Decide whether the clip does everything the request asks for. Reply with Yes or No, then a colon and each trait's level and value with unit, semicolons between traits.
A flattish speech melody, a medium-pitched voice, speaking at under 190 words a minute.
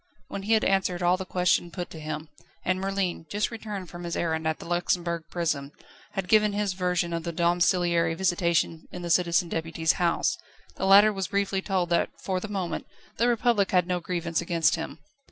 No: narrow, 2.3 semitones; medium, 175 Hz; average, 195 wpm